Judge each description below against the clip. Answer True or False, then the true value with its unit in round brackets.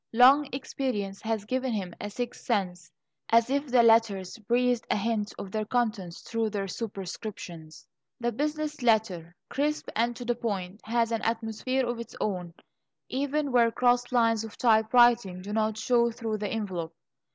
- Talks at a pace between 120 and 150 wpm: False (165 wpm)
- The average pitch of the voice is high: True (225 Hz)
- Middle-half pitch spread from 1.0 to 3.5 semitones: True (3.1 semitones)